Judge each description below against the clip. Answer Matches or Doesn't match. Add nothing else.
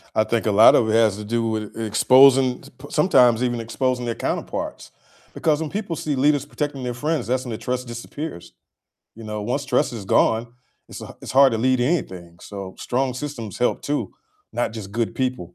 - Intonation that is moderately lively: Matches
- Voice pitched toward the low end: Matches